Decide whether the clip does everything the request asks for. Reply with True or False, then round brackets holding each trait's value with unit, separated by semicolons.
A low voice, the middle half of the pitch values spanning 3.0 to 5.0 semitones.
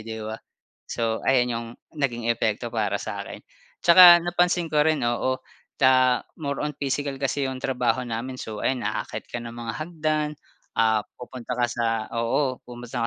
True (130 Hz; 3.9 semitones)